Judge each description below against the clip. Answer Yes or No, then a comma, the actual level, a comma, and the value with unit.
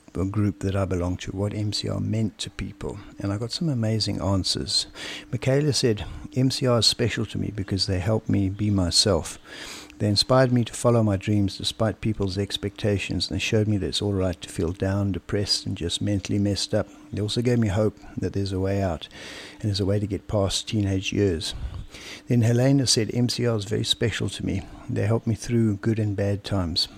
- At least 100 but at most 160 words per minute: No, fast, 205 wpm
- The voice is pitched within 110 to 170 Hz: No, low, 100 Hz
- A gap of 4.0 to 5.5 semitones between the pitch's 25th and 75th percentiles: No, narrow, 2.6 semitones